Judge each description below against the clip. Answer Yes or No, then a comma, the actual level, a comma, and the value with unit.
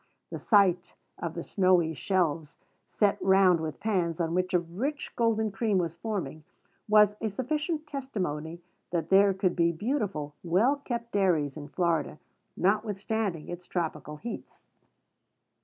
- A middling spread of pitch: Yes, average, 4.5 semitones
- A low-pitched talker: No, medium, 185 Hz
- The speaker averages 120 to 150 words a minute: Yes, average, 140 wpm